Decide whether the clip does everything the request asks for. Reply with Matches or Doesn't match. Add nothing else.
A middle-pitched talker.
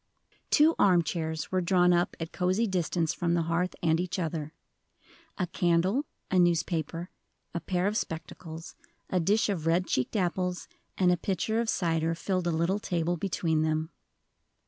Matches